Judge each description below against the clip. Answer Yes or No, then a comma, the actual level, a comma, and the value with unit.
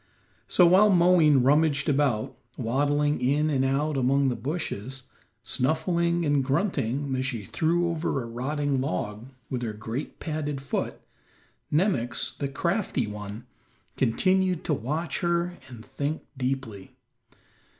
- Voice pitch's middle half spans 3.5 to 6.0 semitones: Yes, average, 4.0 semitones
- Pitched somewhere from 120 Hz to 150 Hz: Yes, medium, 140 Hz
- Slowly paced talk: Yes, slow, 130 wpm